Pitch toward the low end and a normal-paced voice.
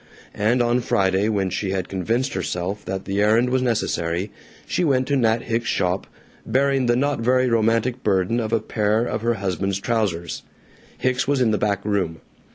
Yes: low, 110 Hz; average, 180 wpm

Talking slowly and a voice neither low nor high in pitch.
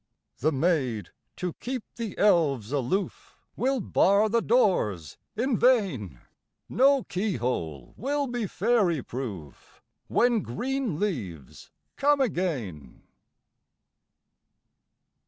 Yes: slow, 100 wpm; medium, 180 Hz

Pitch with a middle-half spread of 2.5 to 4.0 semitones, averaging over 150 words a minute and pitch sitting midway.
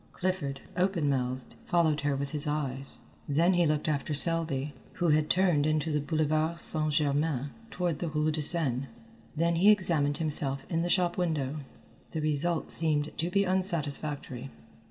Yes: average, 2.9 semitones; average, 160 wpm; medium, 155 Hz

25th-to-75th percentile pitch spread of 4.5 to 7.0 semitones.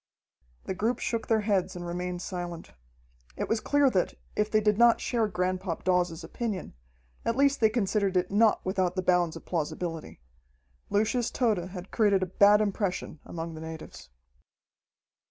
No: average, 3.5 semitones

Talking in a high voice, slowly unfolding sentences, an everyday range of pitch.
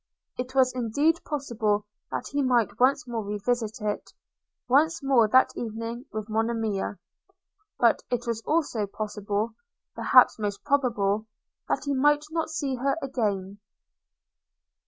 Yes: high, 235 Hz; slow, 130 wpm; average, 4.1 semitones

